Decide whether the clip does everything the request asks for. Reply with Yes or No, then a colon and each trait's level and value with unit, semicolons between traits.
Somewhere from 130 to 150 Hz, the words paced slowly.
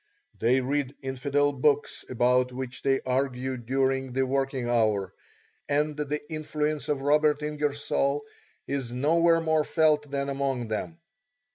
Yes: medium, 140 Hz; slow, 130 wpm